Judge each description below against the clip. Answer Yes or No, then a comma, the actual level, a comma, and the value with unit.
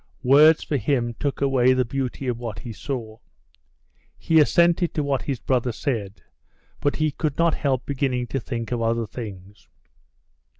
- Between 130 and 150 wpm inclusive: No, average, 165 wpm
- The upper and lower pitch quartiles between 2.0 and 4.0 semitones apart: Yes, average, 3.5 semitones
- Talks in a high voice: No, low, 130 Hz